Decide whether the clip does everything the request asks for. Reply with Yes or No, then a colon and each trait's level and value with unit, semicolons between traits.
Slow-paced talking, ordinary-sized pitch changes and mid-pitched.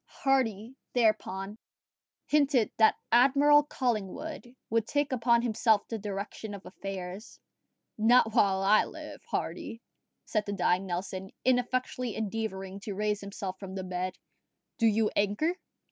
No: slow, 130 wpm; average, 3.9 semitones; high, 215 Hz